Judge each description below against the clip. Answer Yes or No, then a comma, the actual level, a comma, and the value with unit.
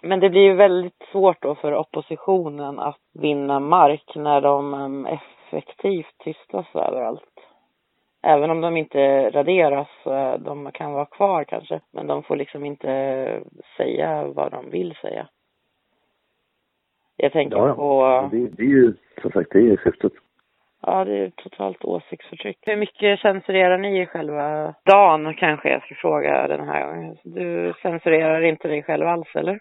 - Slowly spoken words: No, average, 150 wpm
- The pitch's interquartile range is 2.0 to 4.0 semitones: No, average, 4.6 semitones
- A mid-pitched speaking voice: Yes, medium, 150 Hz